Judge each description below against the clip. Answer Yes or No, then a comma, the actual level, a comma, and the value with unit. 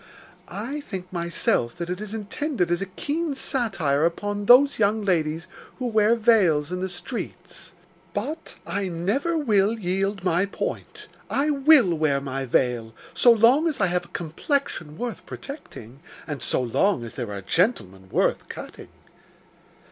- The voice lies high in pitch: Yes, high, 195 Hz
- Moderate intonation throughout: No, wide, 6.7 semitones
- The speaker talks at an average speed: Yes, average, 155 wpm